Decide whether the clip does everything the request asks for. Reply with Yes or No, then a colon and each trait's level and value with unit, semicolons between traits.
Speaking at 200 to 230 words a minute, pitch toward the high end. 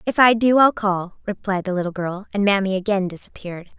Yes: fast, 205 wpm; high, 200 Hz